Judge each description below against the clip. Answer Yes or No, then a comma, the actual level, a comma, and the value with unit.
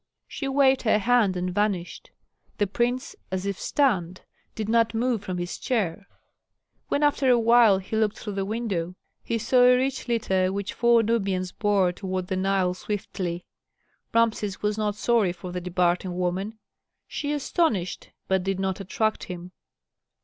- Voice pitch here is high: Yes, high, 205 Hz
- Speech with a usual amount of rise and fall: Yes, average, 3.9 semitones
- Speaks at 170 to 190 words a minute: No, average, 160 wpm